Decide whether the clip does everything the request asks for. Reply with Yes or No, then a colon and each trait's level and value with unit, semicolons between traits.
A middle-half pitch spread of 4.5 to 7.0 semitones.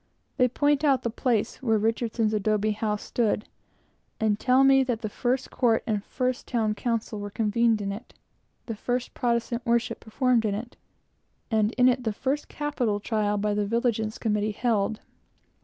No: average, 2.7 semitones